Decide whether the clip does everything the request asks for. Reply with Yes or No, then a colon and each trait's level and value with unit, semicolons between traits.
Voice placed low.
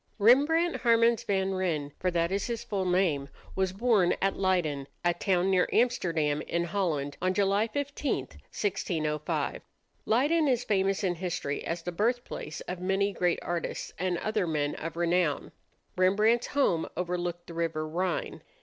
No: medium, 185 Hz